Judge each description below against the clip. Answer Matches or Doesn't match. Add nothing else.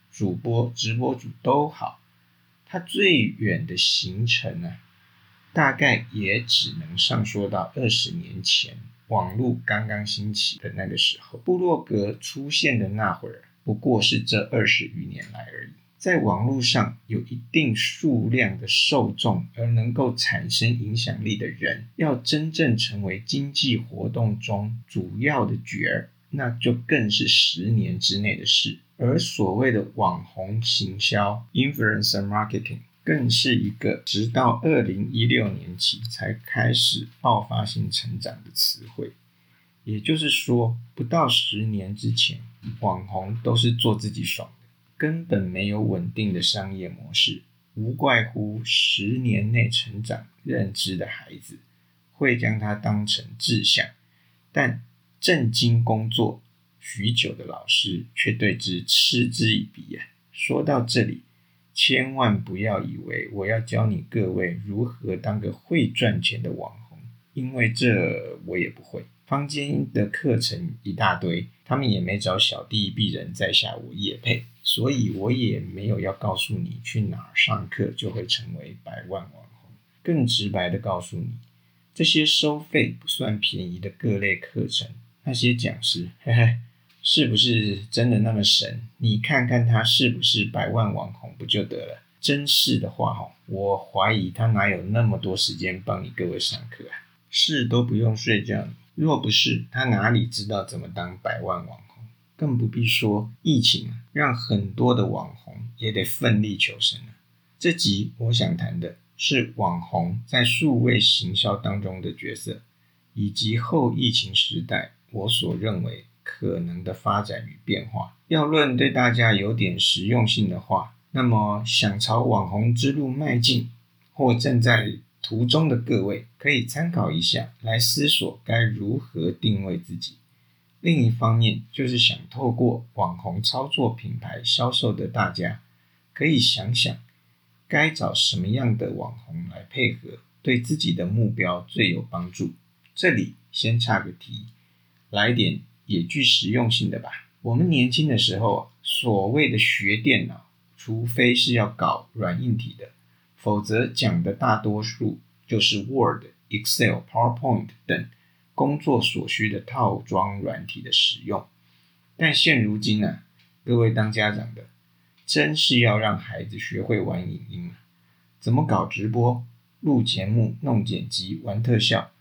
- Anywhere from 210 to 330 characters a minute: Matches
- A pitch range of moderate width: Matches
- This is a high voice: Doesn't match